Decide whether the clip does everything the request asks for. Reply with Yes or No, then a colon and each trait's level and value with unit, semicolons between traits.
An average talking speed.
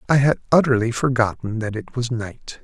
Yes: average, 180 wpm